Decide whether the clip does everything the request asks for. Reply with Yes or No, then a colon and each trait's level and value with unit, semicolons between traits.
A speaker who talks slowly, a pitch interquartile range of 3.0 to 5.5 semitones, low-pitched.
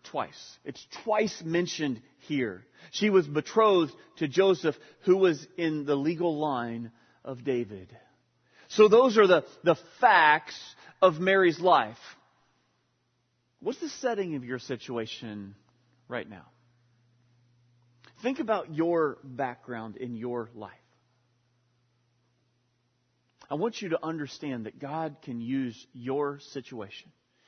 Yes: slow, 115 wpm; average, 5.2 semitones; low, 130 Hz